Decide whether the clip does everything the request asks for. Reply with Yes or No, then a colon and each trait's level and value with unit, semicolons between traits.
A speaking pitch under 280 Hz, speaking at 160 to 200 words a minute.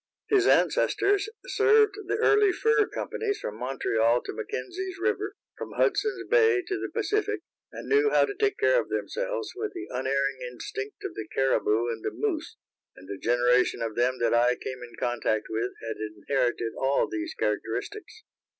No: very high, 355 Hz; average, 170 wpm